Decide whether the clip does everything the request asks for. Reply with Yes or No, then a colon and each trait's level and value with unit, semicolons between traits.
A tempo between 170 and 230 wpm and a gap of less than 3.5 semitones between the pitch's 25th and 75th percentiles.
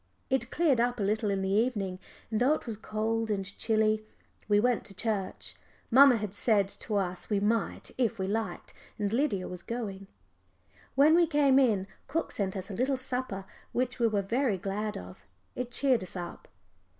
No: average, 185 wpm; average, 4.0 semitones